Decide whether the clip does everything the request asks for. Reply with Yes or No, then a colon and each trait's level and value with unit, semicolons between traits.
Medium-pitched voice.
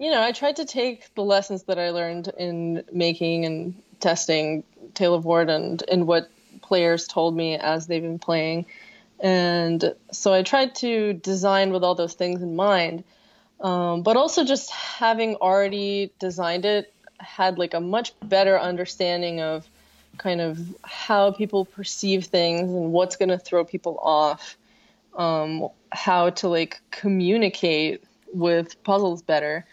Yes: medium, 180 Hz